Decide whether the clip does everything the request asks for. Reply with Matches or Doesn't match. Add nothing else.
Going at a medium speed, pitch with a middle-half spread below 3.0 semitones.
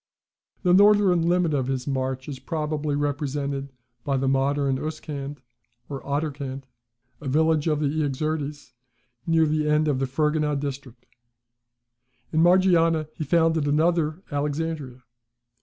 Doesn't match